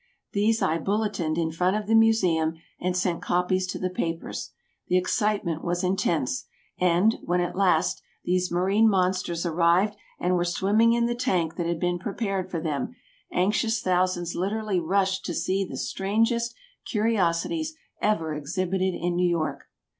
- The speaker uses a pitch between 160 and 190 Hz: Yes, medium, 185 Hz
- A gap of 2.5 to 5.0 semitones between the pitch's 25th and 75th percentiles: Yes, average, 3.2 semitones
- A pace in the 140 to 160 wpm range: Yes, average, 155 wpm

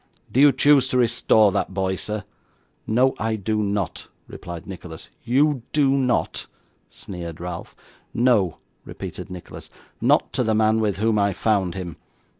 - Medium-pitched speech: No, low, 105 Hz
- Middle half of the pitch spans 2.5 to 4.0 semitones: No, average, 4.6 semitones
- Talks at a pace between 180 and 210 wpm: No, average, 150 wpm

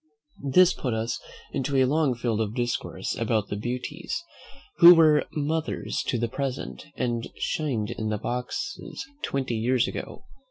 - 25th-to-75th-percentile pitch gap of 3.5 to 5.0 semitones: Yes, average, 4.2 semitones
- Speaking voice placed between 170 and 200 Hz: No, low, 125 Hz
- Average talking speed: Yes, average, 150 wpm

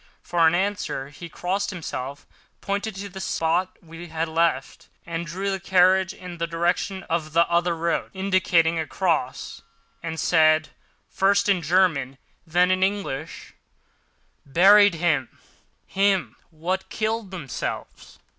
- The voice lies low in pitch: No, medium, 175 Hz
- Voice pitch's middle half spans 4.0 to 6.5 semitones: No, average, 2.8 semitones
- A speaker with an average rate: No, slow, 125 wpm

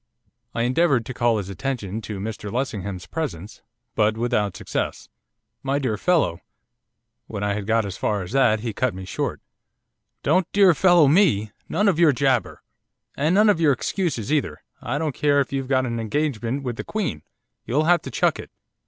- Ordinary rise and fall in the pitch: No, wide, 6.3 semitones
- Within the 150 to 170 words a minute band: No, average, 190 wpm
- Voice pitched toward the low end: Yes, low, 130 Hz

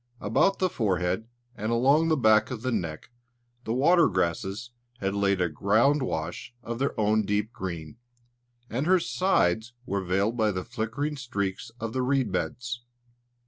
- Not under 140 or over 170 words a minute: Yes, average, 160 wpm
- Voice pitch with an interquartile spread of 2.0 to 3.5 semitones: No, average, 4.6 semitones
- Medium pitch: No, low, 110 Hz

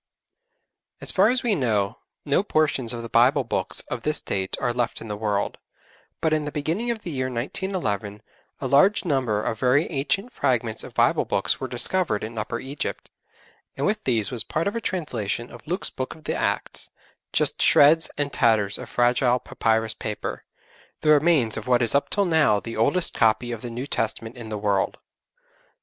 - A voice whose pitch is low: Yes, low, 125 Hz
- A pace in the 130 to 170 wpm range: No, average, 190 wpm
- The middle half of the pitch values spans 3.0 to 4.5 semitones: No, wide, 5.6 semitones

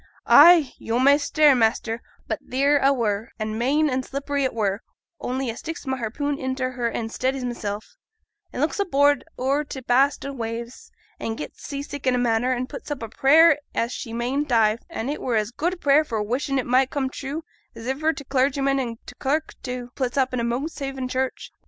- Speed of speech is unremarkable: No, fast, 210 wpm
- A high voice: Yes, very high, 260 Hz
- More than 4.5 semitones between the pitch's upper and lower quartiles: No, average, 3.1 semitones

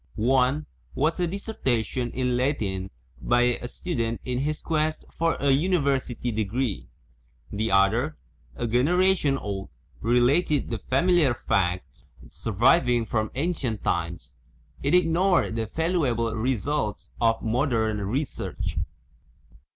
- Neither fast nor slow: No, slow, 130 wpm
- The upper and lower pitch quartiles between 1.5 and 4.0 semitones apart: No, wide, 5.4 semitones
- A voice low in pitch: Yes, low, 125 Hz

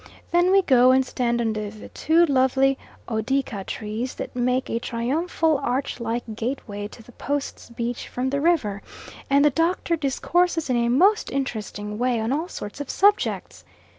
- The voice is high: Yes, very high, 255 Hz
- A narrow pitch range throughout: No, average, 4.0 semitones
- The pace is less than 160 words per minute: No, average, 165 wpm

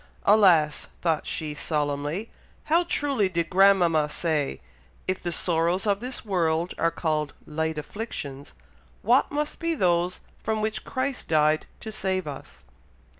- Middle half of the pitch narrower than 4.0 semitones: No, wide, 5.6 semitones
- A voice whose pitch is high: No, medium, 175 Hz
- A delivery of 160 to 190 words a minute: No, slow, 135 wpm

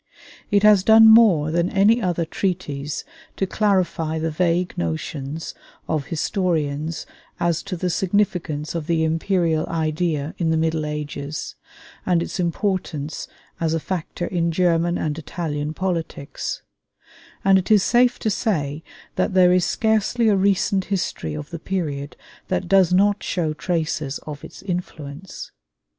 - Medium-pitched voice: Yes, medium, 170 Hz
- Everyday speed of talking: Yes, average, 145 wpm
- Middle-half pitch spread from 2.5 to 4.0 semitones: Yes, average, 3.6 semitones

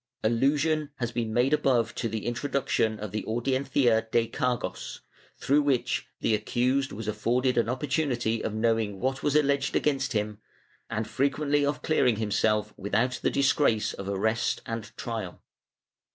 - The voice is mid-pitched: No, low, 120 Hz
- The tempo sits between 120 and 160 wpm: Yes, average, 150 wpm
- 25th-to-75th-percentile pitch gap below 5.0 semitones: Yes, average, 3.8 semitones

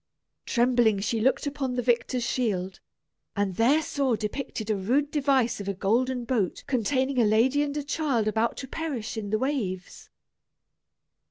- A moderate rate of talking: Yes, average, 160 wpm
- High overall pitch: Yes, high, 240 Hz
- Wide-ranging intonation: No, average, 4.0 semitones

